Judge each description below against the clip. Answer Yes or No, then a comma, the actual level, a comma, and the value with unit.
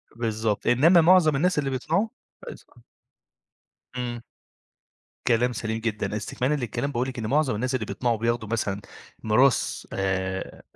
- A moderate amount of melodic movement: Yes, average, 3.9 semitones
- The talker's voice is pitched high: No, low, 120 Hz